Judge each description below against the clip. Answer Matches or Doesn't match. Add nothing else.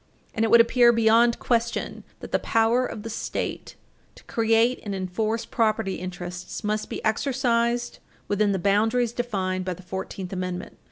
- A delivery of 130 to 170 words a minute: Matches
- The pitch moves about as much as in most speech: Matches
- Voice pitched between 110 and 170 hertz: Doesn't match